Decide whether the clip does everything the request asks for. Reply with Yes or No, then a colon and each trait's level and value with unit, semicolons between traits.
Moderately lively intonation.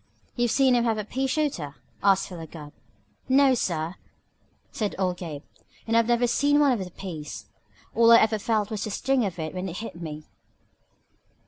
No: wide, 5.9 semitones